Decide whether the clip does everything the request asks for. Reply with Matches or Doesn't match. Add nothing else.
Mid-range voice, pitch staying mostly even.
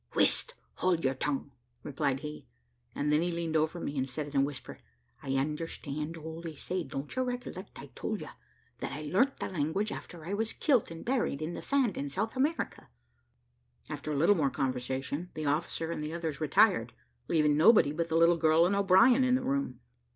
Doesn't match